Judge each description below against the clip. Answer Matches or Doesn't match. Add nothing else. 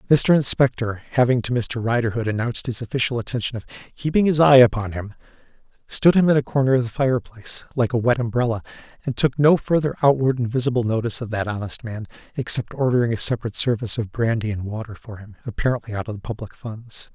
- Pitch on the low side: Matches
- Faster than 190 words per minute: Matches